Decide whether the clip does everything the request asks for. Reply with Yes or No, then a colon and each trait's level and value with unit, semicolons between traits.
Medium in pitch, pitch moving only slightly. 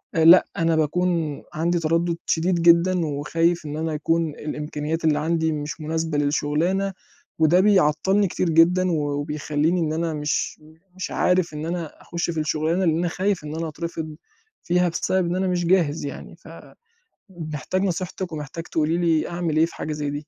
Yes: medium, 165 Hz; narrow, 2.3 semitones